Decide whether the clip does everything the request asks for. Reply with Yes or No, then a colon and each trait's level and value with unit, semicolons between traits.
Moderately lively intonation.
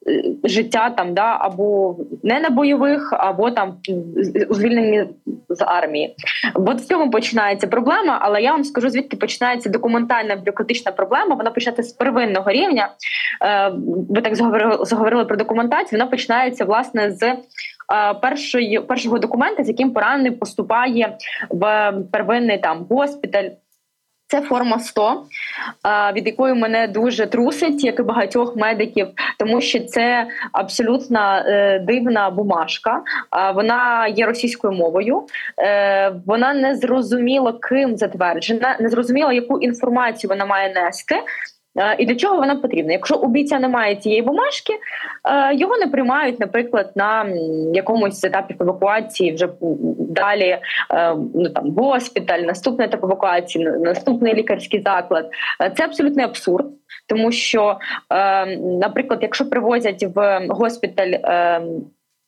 Yes: average, 4.0 semitones